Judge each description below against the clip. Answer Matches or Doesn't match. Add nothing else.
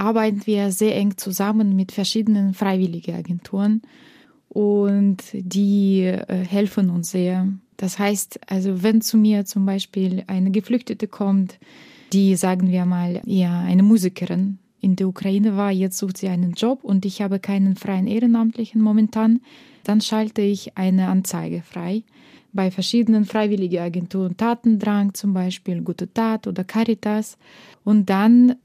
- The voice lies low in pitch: Doesn't match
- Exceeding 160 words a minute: Doesn't match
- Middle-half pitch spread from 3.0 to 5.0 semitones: Doesn't match